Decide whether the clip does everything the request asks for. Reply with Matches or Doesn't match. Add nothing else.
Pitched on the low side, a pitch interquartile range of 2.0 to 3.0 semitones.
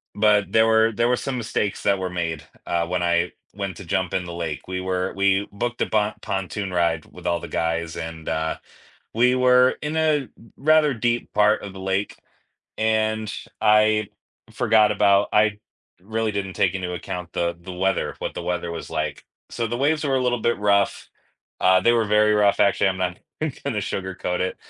Doesn't match